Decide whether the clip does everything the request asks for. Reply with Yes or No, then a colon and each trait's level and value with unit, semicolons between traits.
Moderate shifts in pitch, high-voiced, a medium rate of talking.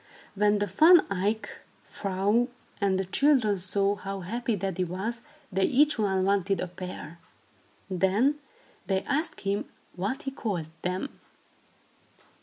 No: average, 3.6 semitones; high, 200 Hz; slow, 130 wpm